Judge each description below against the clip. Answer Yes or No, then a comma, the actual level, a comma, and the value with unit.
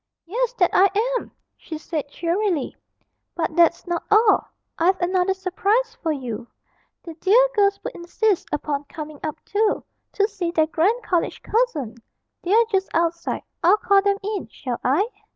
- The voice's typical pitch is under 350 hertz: No, very high, 365 Hz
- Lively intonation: No, average, 4.3 semitones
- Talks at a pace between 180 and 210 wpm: No, average, 155 wpm